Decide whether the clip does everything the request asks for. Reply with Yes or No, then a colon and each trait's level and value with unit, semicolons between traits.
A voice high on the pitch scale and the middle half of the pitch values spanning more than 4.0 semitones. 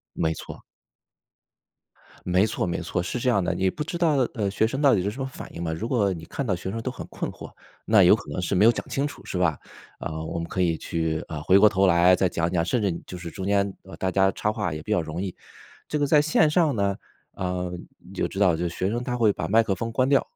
No: very low, 95 Hz; average, 4.7 semitones